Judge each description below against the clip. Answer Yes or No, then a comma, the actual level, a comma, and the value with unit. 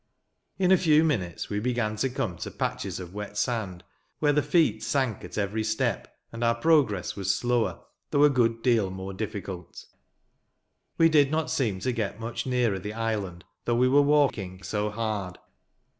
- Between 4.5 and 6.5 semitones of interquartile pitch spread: Yes, average, 4.8 semitones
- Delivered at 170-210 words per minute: Yes, average, 175 wpm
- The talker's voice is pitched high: No, low, 115 Hz